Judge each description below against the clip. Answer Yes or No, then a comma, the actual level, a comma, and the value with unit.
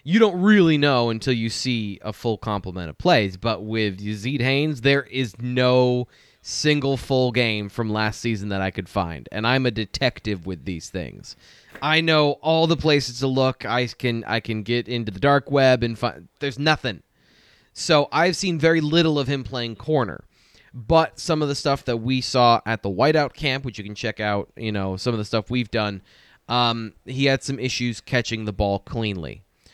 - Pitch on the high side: No, low, 120 Hz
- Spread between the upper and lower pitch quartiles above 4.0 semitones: Yes, average, 4.4 semitones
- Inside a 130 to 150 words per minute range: No, average, 200 wpm